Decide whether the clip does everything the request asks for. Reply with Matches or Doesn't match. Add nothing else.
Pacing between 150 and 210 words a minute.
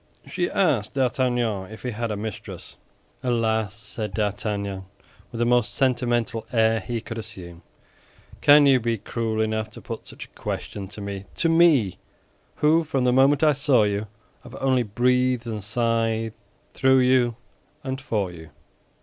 Matches